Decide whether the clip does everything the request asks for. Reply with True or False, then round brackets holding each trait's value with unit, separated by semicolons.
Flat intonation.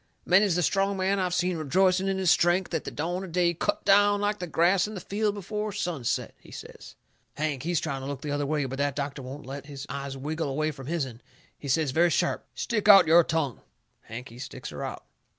False (5.1 semitones)